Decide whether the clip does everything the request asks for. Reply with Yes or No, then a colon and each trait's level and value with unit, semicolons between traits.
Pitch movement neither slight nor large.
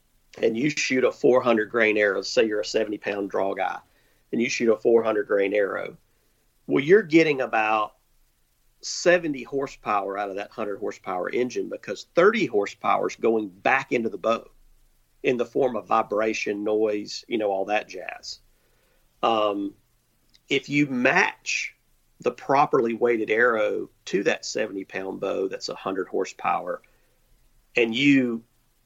No: wide, 5.8 semitones